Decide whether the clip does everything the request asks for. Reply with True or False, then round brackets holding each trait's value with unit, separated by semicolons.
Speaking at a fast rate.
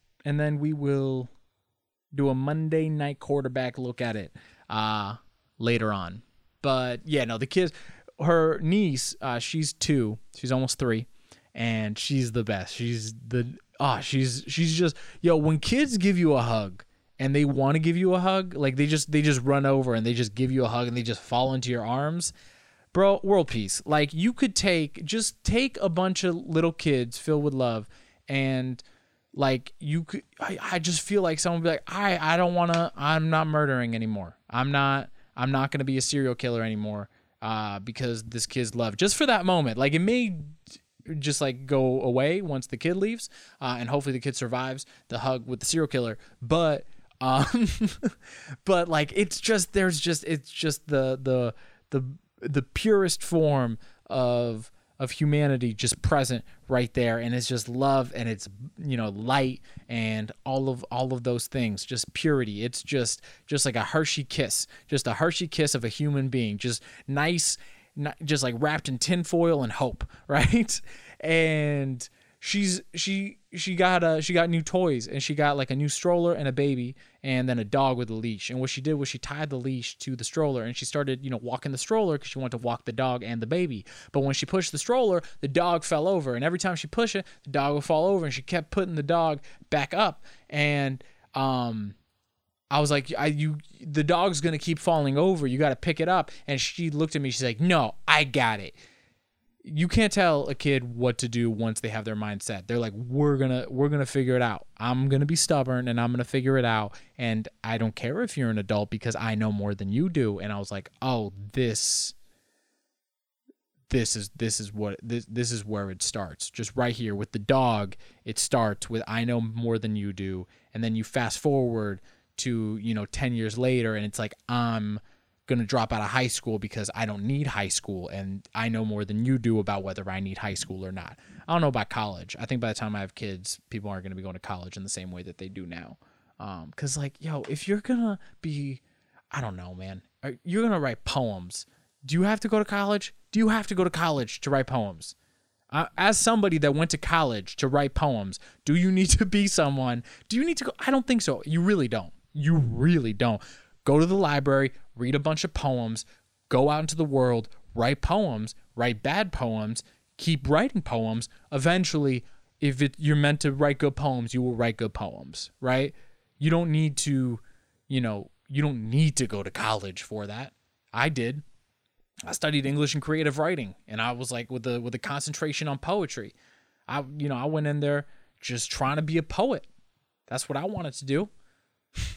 True (215 wpm)